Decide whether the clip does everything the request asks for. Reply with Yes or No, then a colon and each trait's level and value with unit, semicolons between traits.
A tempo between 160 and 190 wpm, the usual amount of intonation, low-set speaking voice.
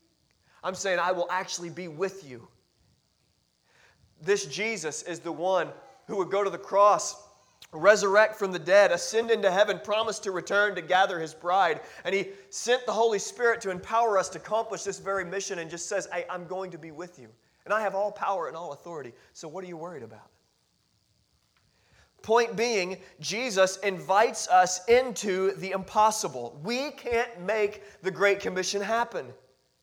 No: average, 175 wpm; average, 3.0 semitones; high, 195 Hz